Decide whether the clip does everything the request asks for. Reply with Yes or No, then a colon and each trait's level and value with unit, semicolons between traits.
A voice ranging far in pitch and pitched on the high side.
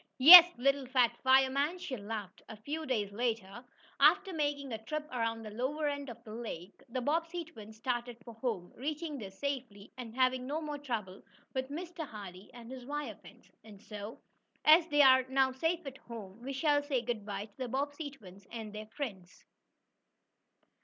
No: average, 4.8 semitones; very high, 255 Hz